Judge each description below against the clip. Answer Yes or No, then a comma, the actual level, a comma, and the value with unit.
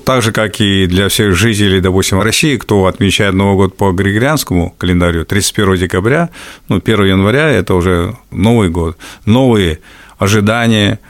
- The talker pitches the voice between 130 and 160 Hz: No, low, 100 Hz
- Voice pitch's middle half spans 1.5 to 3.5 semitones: Yes, average, 3.0 semitones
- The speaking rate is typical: Yes, average, 145 wpm